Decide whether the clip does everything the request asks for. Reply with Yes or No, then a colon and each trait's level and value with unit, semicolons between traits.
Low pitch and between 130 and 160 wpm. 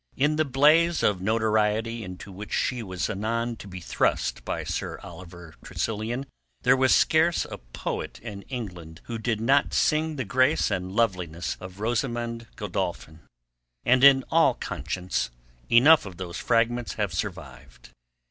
Yes: low, 110 Hz; average, 150 wpm